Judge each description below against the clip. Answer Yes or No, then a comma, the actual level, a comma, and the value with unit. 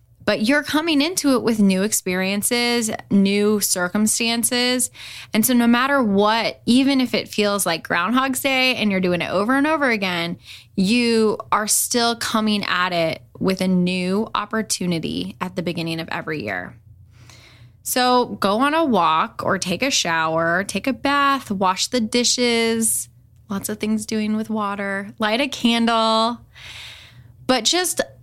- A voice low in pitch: No, high, 215 Hz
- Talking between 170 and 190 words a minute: No, average, 155 wpm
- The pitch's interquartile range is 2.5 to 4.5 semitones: No, average, 5.1 semitones